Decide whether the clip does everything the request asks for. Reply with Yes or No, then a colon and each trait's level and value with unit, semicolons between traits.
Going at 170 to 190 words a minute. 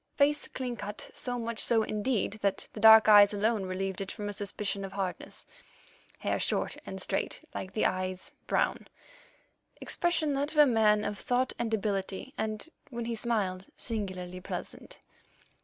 No: average, 155 wpm